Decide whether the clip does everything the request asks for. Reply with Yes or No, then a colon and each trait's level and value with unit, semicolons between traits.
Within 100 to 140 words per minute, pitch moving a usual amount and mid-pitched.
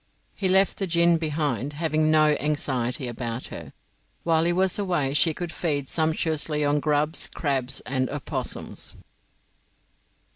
Yes: slow, 135 wpm; average, 3.1 semitones; medium, 150 Hz